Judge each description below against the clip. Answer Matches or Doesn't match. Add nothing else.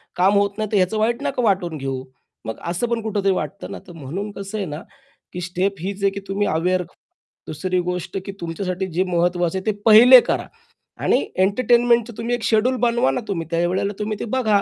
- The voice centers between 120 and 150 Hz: Doesn't match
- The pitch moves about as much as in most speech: Matches